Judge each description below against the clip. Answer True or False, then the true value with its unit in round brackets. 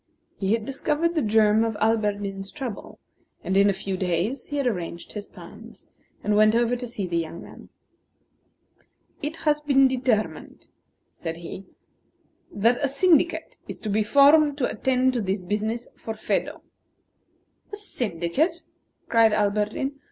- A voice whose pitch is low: False (225 Hz)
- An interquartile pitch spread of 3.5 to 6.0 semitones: True (5.2 semitones)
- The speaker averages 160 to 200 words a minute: False (150 wpm)